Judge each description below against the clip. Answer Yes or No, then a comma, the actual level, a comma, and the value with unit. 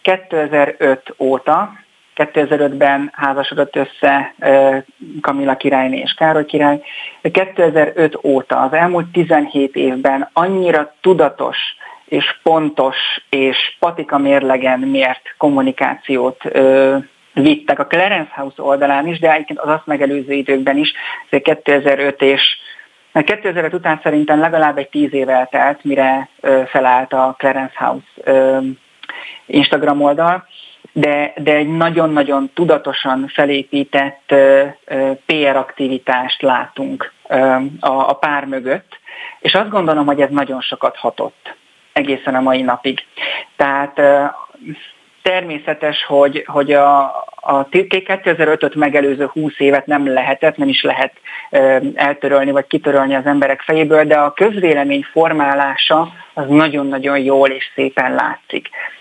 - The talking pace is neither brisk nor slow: Yes, average, 125 wpm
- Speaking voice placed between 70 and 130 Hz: No, medium, 140 Hz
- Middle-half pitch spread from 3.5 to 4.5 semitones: No, narrow, 2.5 semitones